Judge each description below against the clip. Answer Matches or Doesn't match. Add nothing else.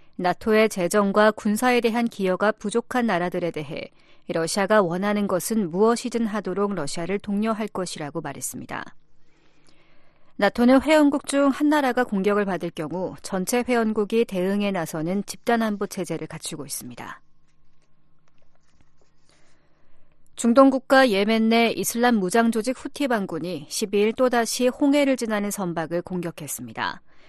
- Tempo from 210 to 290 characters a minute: Doesn't match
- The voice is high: Matches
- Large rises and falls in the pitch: Doesn't match